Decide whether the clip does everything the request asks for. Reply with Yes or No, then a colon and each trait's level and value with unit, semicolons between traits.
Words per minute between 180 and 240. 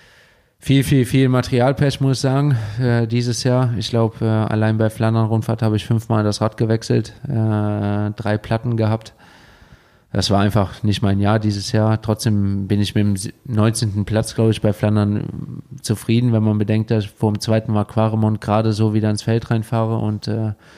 Yes: average, 185 wpm